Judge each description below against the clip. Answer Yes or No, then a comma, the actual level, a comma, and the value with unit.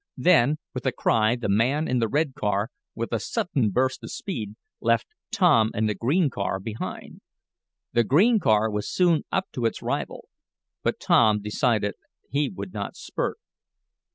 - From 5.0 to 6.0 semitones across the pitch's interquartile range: Yes, wide, 5.4 semitones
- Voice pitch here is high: No, low, 120 Hz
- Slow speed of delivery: No, average, 165 wpm